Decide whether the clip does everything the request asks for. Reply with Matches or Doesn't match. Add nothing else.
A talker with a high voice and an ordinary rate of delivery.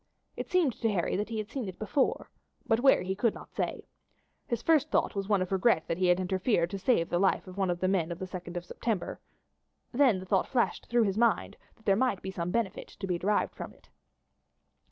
Doesn't match